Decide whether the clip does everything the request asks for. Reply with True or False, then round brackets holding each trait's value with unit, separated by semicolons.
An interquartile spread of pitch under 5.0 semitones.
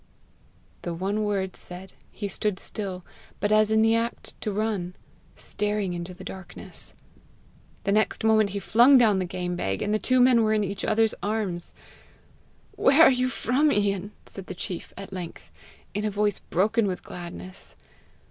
True (2.9 semitones)